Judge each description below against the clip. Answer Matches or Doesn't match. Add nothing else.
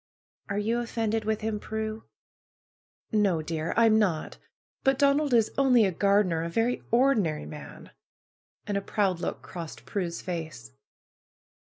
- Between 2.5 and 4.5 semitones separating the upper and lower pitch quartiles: Doesn't match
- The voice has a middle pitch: Doesn't match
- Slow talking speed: Doesn't match